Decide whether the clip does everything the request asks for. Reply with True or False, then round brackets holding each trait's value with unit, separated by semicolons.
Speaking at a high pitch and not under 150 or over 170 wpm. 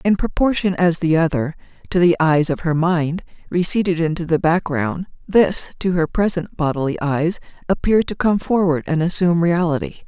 False (170 Hz; 165 wpm)